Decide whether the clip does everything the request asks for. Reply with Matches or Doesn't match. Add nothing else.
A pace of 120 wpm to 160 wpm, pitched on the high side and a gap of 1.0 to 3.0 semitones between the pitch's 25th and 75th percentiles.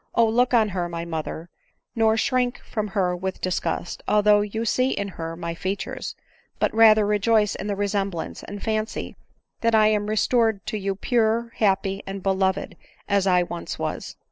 Doesn't match